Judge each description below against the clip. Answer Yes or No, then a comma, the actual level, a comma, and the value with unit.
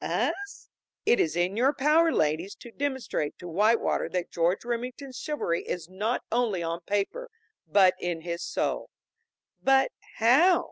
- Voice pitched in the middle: No, high, 220 Hz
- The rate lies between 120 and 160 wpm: Yes, average, 145 wpm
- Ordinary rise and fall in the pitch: No, wide, 7.3 semitones